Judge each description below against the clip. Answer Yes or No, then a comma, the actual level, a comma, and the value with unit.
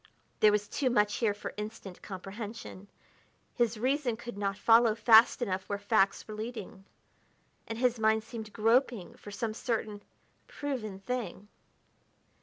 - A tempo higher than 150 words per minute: No, average, 140 wpm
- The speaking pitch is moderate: No, high, 220 Hz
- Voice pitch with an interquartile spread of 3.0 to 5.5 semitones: No, narrow, 2.5 semitones